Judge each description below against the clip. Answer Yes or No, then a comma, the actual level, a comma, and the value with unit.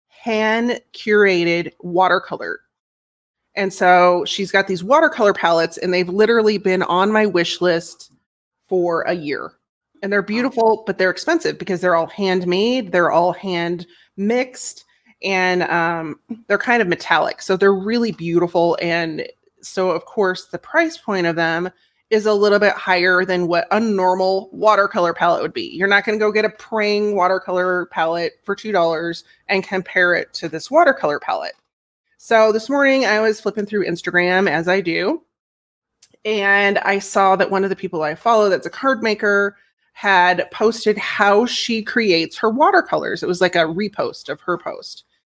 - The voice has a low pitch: No, high, 195 Hz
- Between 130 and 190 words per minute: Yes, average, 165 wpm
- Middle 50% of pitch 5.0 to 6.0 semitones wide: No, average, 3.3 semitones